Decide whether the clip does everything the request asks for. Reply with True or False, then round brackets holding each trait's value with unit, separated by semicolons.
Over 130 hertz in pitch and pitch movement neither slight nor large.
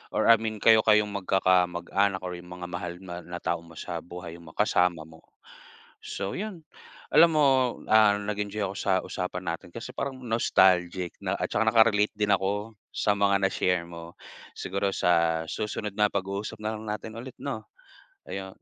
False (100 Hz; 3.3 semitones)